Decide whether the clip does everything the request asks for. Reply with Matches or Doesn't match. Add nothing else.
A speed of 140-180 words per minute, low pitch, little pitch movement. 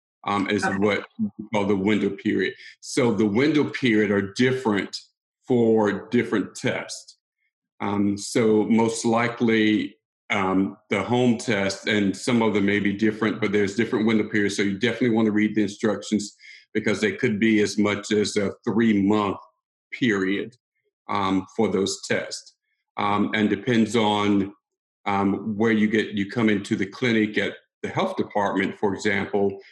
Matches